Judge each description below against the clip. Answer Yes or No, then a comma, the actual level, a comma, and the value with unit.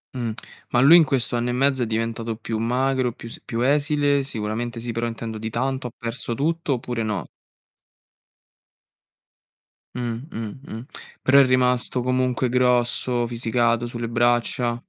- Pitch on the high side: No, low, 120 Hz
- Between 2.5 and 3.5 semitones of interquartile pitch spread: No, narrow, 1.9 semitones